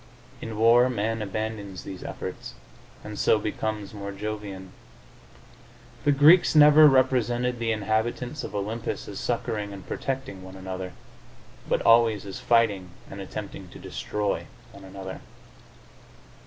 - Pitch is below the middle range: Yes, low, 110 Hz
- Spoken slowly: Yes, slow, 130 wpm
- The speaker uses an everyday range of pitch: Yes, average, 3.3 semitones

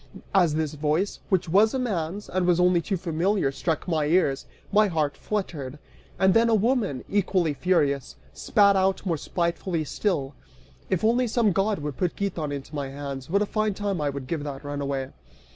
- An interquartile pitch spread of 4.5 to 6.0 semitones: Yes, wide, 5.4 semitones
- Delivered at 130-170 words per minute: No, average, 185 wpm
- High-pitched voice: No, medium, 175 Hz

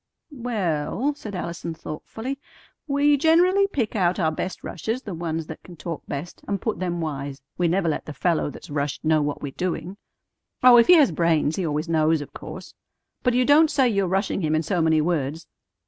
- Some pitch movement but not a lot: No, wide, 6.9 semitones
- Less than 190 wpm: No, average, 200 wpm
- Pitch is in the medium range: Yes, medium, 175 Hz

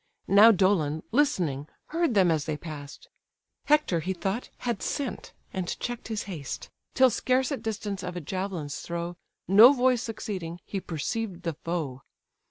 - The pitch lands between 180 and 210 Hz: Yes, high, 190 Hz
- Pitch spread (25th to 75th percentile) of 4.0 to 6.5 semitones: Yes, wide, 5.4 semitones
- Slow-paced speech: No, average, 155 wpm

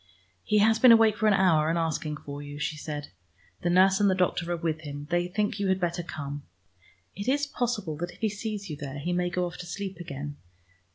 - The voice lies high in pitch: No, medium, 175 Hz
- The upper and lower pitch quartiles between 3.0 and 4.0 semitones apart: No, average, 4.8 semitones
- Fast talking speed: Yes, fast, 235 wpm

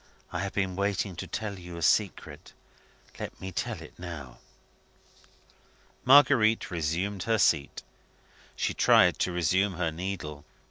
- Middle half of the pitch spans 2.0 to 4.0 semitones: Yes, average, 3.2 semitones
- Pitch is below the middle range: Yes, very low, 95 Hz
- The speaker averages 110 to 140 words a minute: Yes, slow, 135 wpm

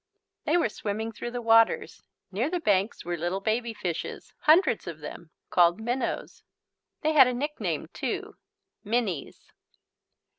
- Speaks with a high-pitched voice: Yes, high, 225 Hz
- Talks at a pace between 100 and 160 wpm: Yes, average, 140 wpm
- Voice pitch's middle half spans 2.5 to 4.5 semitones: No, average, 4.9 semitones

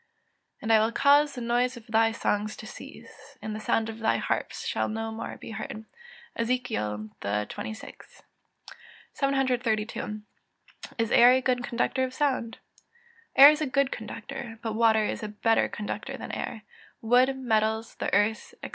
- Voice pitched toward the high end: Yes, high, 225 Hz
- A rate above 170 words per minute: No, average, 165 wpm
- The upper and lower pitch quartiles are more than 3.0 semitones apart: No, narrow, 2.6 semitones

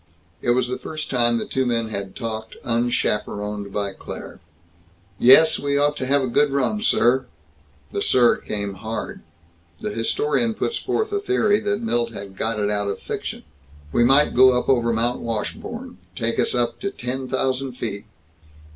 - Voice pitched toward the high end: No, low, 120 Hz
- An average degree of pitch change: Yes, average, 4.2 semitones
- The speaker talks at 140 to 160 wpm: No, average, 175 wpm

